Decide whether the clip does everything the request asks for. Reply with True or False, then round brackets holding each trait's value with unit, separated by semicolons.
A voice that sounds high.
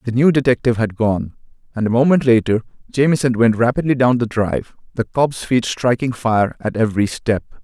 False (120 Hz)